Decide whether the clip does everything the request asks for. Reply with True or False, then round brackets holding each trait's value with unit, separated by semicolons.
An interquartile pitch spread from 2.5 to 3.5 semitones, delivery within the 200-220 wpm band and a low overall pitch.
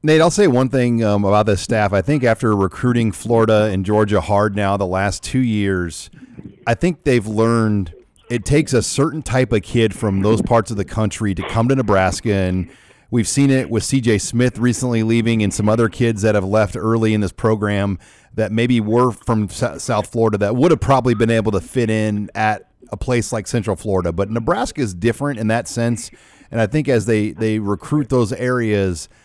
True (2.9 semitones; 205 wpm; 110 Hz)